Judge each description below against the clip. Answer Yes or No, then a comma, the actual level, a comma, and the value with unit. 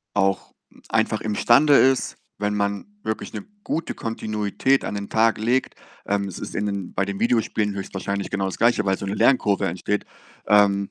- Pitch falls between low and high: No, low, 105 Hz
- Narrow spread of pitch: Yes, narrow, 2.2 semitones